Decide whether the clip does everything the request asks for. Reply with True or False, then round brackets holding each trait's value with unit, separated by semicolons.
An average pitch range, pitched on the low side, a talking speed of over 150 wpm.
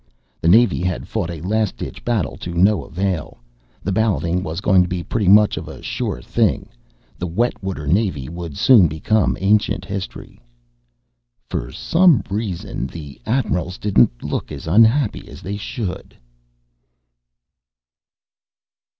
False (4.0 semitones; 95 Hz; 140 wpm)